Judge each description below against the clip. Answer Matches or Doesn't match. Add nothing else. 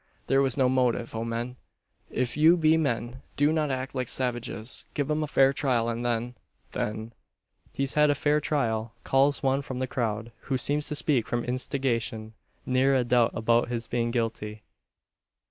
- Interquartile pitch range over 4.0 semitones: Doesn't match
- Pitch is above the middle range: Doesn't match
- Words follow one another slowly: Doesn't match